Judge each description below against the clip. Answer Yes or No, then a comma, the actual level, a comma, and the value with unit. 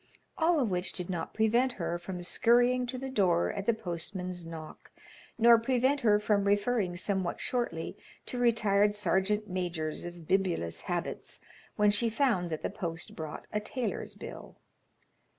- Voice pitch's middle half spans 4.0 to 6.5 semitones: Yes, average, 5.2 semitones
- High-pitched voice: Yes, high, 200 Hz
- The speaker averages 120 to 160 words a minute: Yes, average, 155 wpm